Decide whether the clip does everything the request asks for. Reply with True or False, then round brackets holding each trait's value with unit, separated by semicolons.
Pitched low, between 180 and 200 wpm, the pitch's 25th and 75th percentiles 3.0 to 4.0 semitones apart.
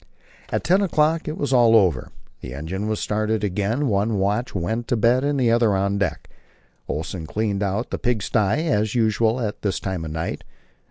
True (110 Hz; 185 wpm; 3.6 semitones)